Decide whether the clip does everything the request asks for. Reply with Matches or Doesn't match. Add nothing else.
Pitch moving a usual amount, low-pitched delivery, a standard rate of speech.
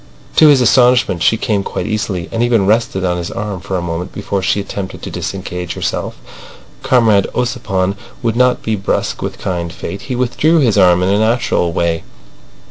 Matches